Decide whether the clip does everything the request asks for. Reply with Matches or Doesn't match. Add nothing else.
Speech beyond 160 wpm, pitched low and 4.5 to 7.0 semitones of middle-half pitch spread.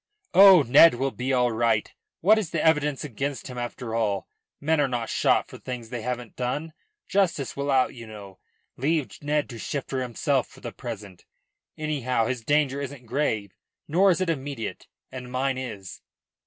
Doesn't match